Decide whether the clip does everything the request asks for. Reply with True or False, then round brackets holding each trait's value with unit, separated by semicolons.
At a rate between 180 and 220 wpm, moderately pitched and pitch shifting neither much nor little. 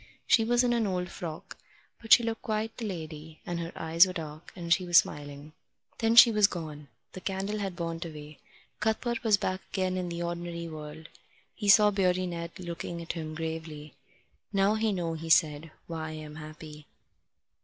True (185 wpm; 170 Hz; 3.9 semitones)